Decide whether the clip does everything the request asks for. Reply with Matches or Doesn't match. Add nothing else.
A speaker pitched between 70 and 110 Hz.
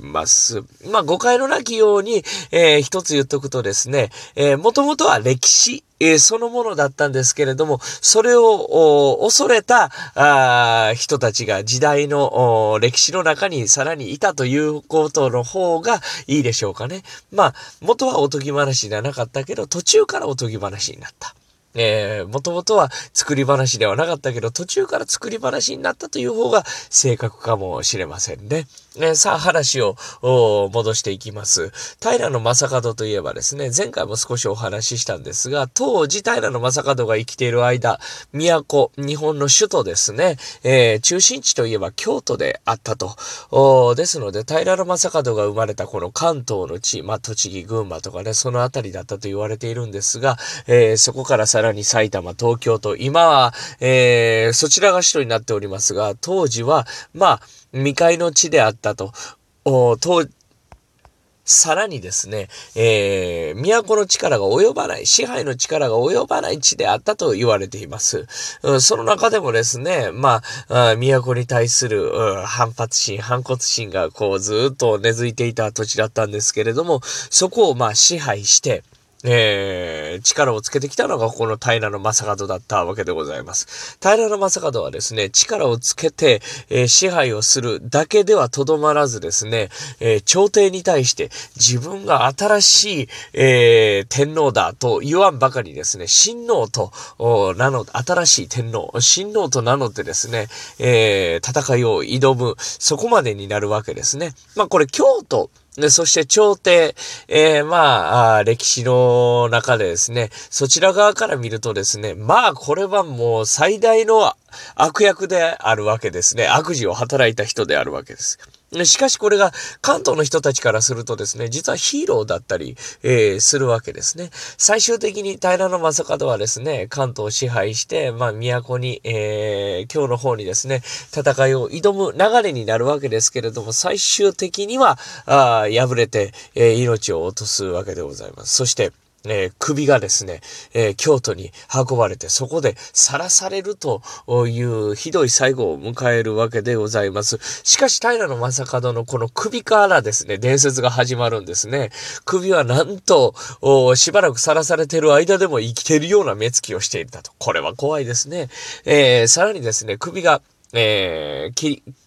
Doesn't match